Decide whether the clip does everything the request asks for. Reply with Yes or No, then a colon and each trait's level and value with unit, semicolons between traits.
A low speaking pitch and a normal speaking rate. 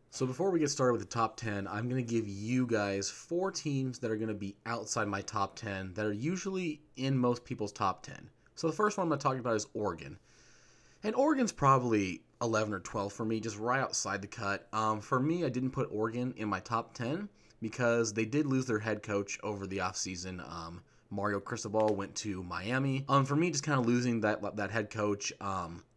No: low, 115 Hz; fast, 220 wpm